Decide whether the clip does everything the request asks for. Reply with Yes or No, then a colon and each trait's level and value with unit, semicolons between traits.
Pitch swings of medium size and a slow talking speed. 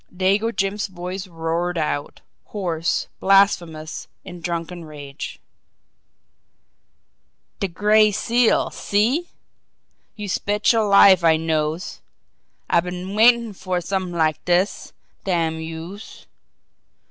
Yes: average, 3.6 semitones; slow, 100 wpm